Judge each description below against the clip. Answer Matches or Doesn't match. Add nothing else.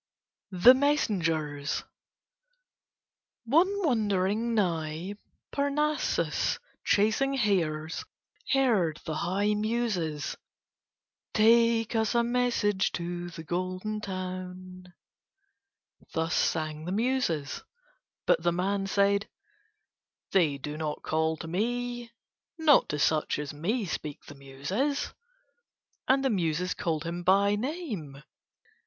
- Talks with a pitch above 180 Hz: Matches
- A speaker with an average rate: Doesn't match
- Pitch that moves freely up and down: Matches